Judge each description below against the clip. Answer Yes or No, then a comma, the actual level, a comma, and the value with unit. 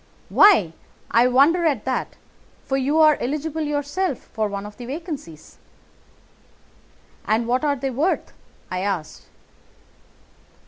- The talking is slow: Yes, slow, 125 wpm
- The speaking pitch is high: Yes, very high, 270 Hz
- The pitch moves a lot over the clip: Yes, wide, 5.8 semitones